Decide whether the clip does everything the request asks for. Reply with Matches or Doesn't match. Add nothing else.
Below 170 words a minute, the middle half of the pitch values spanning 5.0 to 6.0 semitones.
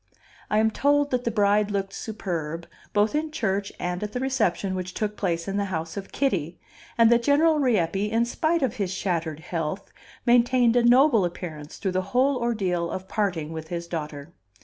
Doesn't match